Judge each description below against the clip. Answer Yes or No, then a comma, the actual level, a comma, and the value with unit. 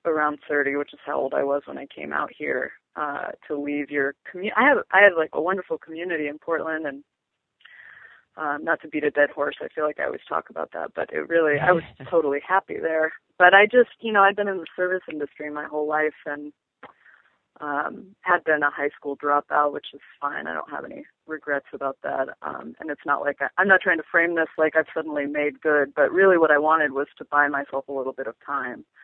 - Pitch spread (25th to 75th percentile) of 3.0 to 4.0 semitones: Yes, average, 3.4 semitones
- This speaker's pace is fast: Yes, fast, 240 wpm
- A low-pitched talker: No, medium, 150 Hz